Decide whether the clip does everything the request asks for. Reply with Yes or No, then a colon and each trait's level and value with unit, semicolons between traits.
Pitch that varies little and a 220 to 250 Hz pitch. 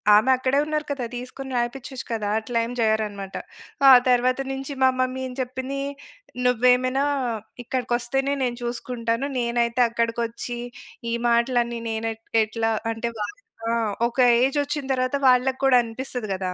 Yes: narrow, 2.2 semitones; high, 245 Hz